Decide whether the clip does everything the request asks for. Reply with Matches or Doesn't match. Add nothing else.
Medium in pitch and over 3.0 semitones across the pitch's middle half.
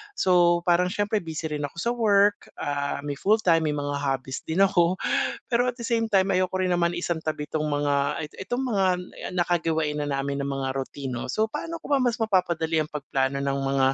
Matches